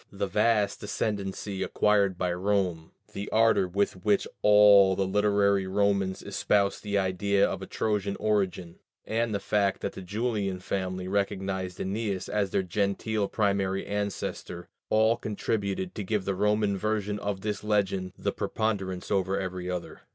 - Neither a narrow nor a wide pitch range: No, narrow, 1.7 semitones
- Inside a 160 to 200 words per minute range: No, average, 150 wpm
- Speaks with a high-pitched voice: No, low, 100 Hz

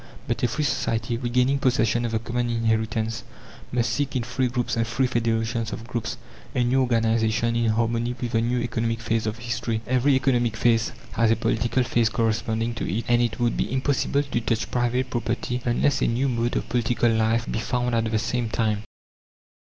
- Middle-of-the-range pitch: No, low, 115 Hz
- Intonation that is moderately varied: No, narrow, 1.4 semitones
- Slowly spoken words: No, average, 195 wpm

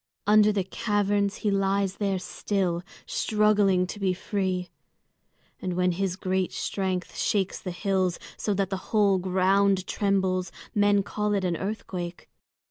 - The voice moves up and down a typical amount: No, narrow, 1.8 semitones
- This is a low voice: No, high, 195 Hz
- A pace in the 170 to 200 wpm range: No, average, 140 wpm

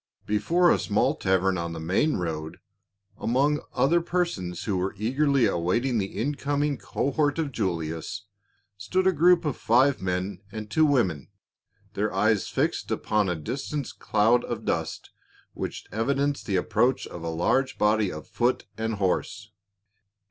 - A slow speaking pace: No, average, 150 wpm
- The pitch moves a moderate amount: No, wide, 7.3 semitones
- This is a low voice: Yes, low, 110 Hz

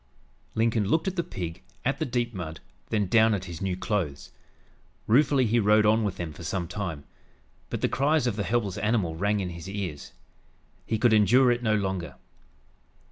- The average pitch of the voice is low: Yes, low, 105 Hz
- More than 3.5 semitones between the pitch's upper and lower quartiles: Yes, average, 4.6 semitones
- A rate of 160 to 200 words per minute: Yes, average, 190 wpm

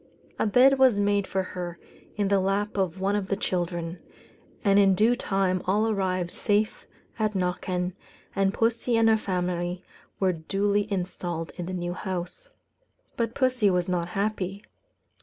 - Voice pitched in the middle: No, high, 195 Hz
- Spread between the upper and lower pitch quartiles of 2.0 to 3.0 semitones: Yes, narrow, 2.6 semitones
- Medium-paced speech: Yes, average, 160 wpm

